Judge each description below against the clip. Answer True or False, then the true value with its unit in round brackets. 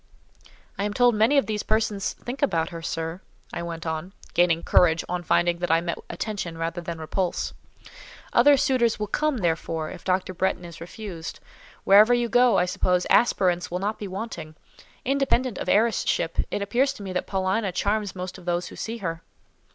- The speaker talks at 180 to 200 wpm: True (190 wpm)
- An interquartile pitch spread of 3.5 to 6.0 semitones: True (4.4 semitones)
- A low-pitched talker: False (185 Hz)